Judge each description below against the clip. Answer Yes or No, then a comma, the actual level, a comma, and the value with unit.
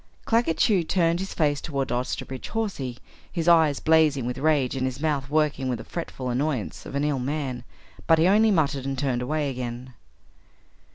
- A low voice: No, medium, 145 Hz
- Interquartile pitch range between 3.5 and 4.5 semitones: Yes, average, 3.8 semitones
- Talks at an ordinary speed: Yes, average, 180 wpm